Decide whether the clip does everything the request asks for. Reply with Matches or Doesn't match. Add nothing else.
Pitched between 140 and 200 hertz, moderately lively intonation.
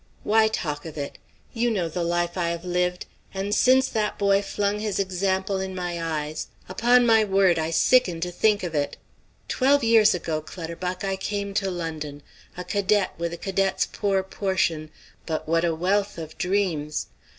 Matches